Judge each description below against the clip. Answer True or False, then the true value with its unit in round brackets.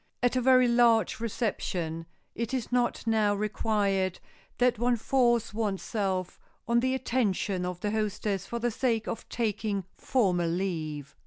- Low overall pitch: False (215 Hz)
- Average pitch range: True (3.8 semitones)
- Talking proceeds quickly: False (150 wpm)